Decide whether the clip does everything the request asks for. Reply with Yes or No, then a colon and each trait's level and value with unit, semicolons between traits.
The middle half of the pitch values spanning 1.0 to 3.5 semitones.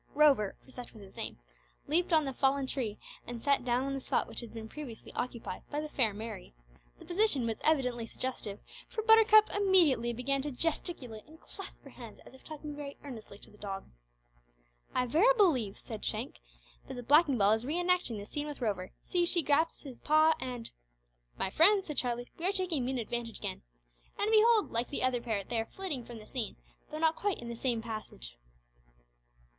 No: wide, 5.5 semitones